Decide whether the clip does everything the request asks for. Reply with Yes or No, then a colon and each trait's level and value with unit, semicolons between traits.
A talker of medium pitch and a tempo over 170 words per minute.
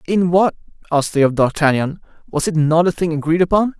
Yes: medium, 165 Hz; fast, 205 wpm